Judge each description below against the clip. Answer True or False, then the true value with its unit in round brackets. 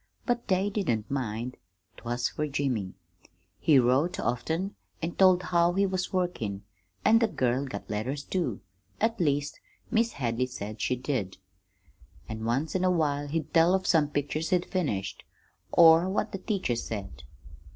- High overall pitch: False (145 Hz)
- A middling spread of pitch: False (7.2 semitones)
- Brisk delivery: False (160 wpm)